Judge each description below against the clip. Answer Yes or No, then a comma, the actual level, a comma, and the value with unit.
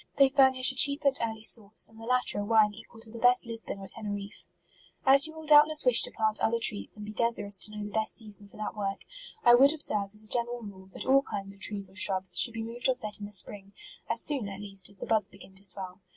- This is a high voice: Yes, high, 215 Hz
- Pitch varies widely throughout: No, average, 3.4 semitones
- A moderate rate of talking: No, fast, 270 wpm